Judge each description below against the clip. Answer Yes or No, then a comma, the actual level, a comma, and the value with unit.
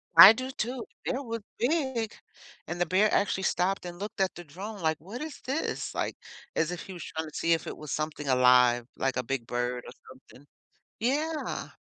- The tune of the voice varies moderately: No, wide, 7.6 semitones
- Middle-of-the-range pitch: Yes, medium, 180 Hz